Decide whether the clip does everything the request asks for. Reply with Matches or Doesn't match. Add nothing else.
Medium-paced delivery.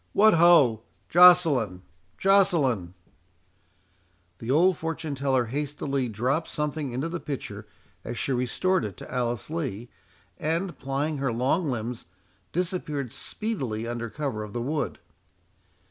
Doesn't match